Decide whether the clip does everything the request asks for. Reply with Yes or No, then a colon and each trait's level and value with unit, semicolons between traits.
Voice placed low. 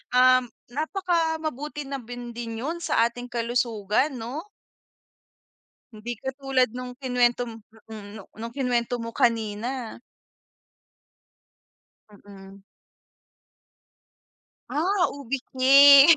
No: very high, 250 Hz